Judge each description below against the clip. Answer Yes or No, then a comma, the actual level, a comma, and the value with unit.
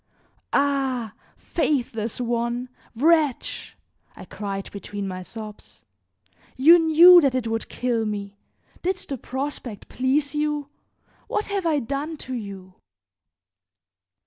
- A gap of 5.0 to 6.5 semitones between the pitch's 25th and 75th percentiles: Yes, average, 5.3 semitones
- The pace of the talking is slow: Yes, slow, 115 wpm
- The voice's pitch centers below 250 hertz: No, very high, 255 Hz